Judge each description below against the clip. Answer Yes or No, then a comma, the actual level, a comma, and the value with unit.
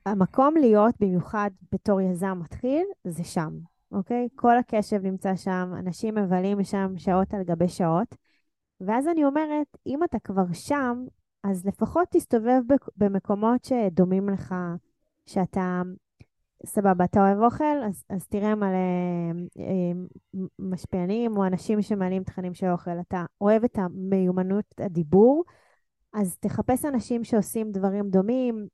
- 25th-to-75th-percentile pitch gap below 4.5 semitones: Yes, average, 4.1 semitones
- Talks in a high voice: Yes, high, 200 Hz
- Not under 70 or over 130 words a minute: Yes, average, 125 wpm